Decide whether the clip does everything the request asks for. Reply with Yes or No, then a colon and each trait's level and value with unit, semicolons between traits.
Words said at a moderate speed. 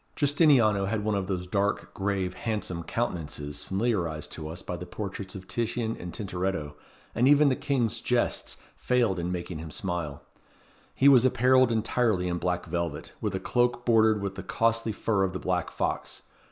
Yes: average, 175 wpm